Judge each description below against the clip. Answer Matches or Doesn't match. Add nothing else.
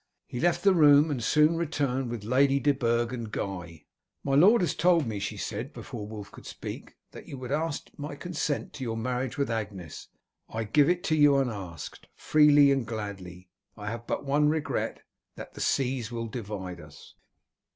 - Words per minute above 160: Matches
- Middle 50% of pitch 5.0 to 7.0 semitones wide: Matches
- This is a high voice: Doesn't match